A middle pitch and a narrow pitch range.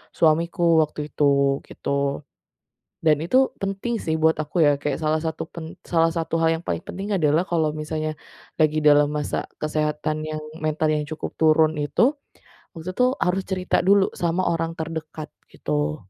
Yes: medium, 155 Hz; narrow, 1.9 semitones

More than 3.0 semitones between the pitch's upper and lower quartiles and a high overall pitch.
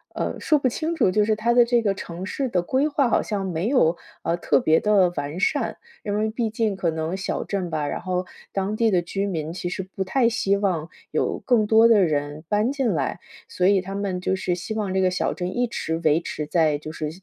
Yes: average, 4.2 semitones; high, 195 Hz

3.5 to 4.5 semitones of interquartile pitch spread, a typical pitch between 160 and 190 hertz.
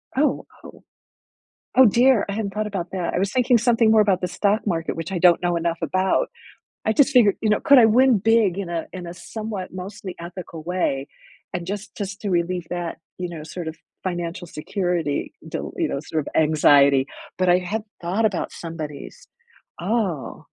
Yes: average, 3.9 semitones; medium, 185 Hz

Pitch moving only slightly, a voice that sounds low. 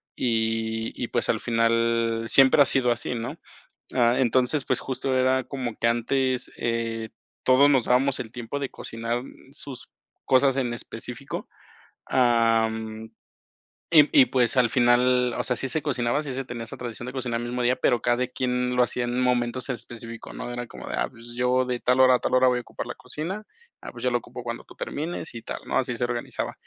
Yes: narrow, 1.8 semitones; low, 125 Hz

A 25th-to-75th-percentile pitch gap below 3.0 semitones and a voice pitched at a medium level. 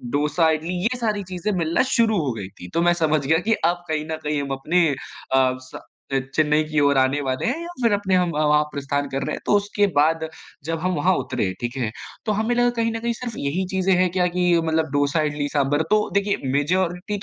No: average, 4.8 semitones; medium, 160 Hz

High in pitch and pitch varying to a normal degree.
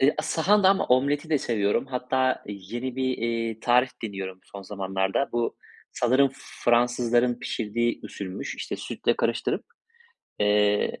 No: low, 120 Hz; average, 4.0 semitones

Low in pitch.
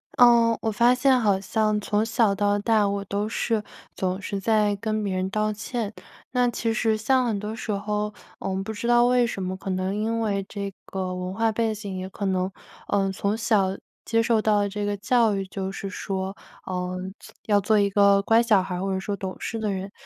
No: high, 205 Hz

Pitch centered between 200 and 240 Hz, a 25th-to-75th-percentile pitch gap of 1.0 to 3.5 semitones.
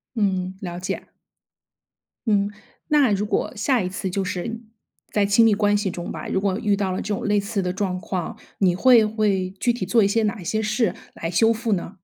Yes: high, 205 Hz; average, 2.8 semitones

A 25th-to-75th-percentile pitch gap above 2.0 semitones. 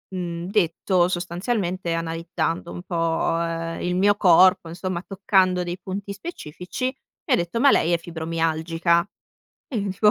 Yes: narrow, 2.4 semitones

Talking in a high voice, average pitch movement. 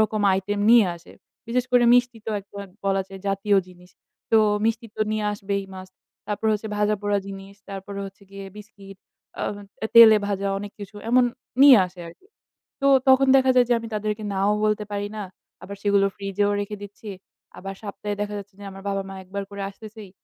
No: high, 205 Hz; narrow, 1.7 semitones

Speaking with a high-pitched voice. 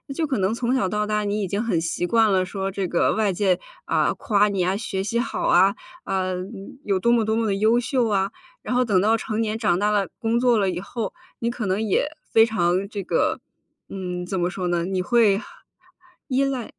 Yes: high, 205 Hz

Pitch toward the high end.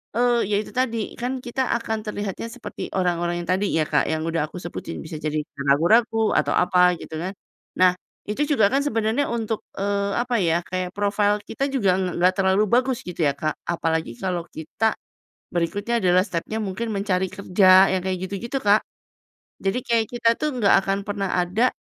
Yes: high, 200 Hz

